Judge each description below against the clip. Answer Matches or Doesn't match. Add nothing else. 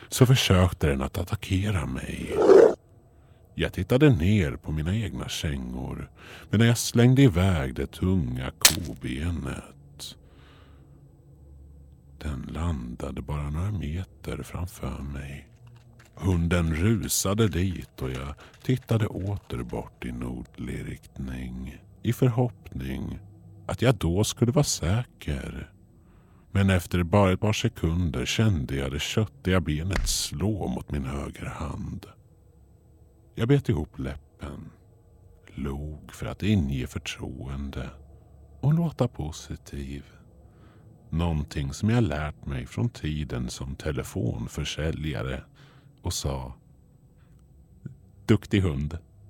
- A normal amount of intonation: Doesn't match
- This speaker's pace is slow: Matches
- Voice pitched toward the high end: Doesn't match